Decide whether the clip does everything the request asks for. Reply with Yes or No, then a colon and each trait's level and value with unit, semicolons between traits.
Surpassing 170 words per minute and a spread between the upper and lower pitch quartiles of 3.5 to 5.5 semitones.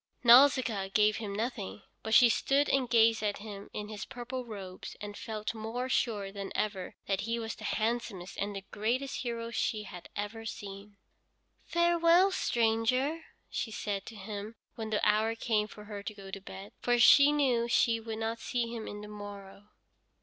No: average, 180 wpm; narrow, 2.6 semitones